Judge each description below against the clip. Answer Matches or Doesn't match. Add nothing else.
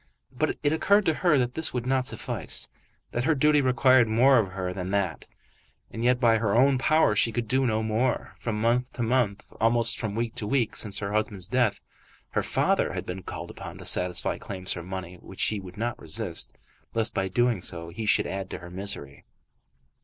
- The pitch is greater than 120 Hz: Doesn't match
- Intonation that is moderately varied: Matches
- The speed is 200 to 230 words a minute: Matches